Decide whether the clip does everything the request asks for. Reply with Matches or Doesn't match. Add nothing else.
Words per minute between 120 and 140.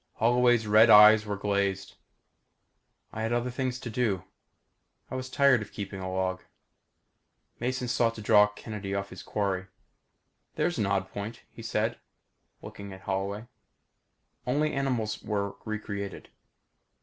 Matches